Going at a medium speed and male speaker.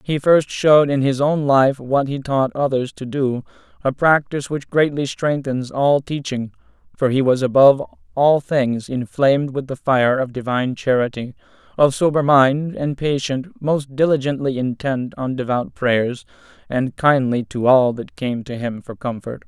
Yes: average, 165 wpm; male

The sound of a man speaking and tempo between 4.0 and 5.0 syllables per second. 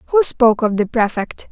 No: female; 4.8 syllables/s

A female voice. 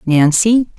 Yes: female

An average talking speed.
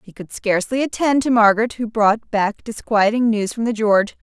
Yes: average, 195 wpm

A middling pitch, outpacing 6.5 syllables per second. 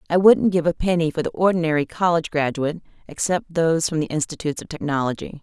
Yes: medium, 165 Hz; 6.7 syllables/s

